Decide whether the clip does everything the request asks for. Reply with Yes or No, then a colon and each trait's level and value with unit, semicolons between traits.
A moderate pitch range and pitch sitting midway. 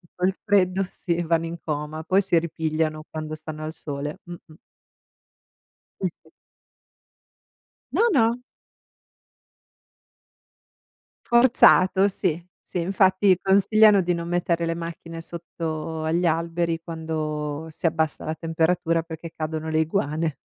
No: narrow, 2.3 semitones; medium, 165 Hz